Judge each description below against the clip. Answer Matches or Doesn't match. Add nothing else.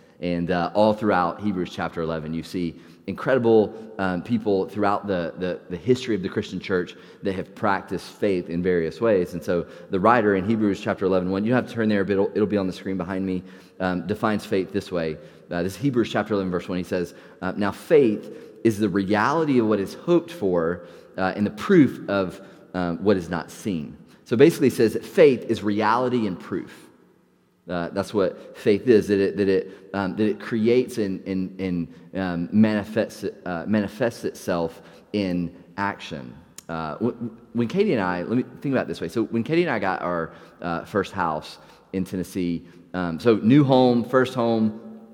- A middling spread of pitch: Matches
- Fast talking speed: Doesn't match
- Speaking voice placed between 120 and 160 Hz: Doesn't match